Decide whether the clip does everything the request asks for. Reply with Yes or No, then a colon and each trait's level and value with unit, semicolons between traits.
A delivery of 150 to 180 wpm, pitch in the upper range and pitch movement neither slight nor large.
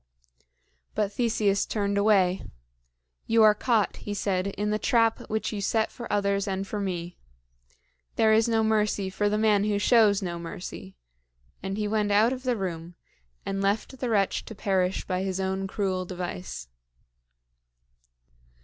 No: average, 160 wpm; high, 200 Hz; narrow, 2.2 semitones